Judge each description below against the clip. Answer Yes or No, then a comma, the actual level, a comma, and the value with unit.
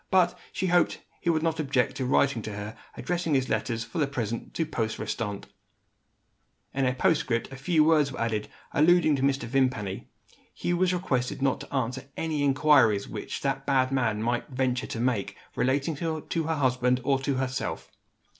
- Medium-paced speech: Yes, average, 185 wpm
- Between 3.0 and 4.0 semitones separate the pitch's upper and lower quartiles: Yes, average, 3.7 semitones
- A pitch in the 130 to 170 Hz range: Yes, low, 135 Hz